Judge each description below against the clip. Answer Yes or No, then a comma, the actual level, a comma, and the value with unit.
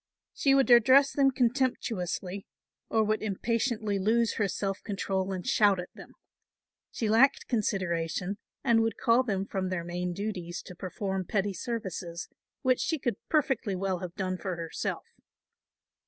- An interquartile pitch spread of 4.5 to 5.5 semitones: No, average, 4.1 semitones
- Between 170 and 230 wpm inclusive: No, average, 150 wpm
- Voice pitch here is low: No, high, 200 Hz